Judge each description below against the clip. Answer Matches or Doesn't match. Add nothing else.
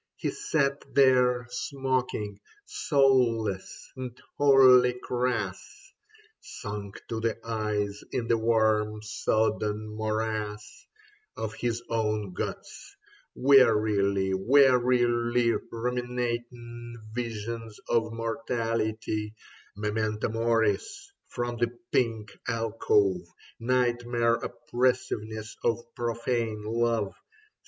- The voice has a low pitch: Matches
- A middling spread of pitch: Doesn't match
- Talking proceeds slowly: Matches